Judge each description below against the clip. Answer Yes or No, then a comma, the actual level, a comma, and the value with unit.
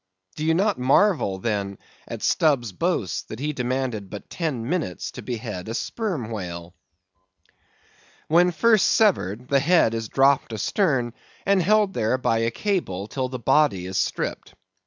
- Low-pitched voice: Yes, low, 130 Hz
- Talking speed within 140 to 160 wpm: Yes, average, 155 wpm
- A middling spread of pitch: No, wide, 7.6 semitones